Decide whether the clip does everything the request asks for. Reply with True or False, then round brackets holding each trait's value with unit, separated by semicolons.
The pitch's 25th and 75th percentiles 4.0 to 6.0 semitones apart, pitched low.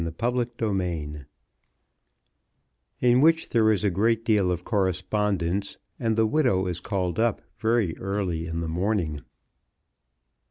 True (4.3 semitones; 100 Hz)